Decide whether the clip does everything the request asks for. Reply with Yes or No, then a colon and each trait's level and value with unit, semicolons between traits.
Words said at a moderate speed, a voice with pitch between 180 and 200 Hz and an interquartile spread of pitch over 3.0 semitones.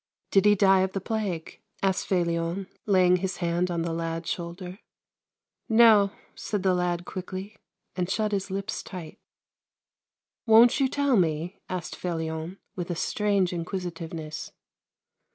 No: average, 155 wpm; medium, 185 Hz; average, 2.7 semitones